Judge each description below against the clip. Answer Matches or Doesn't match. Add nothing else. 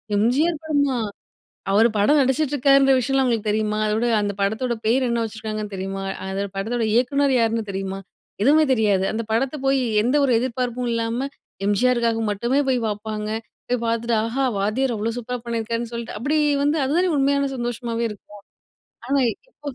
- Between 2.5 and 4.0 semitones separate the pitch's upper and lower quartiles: Matches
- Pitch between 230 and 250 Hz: Matches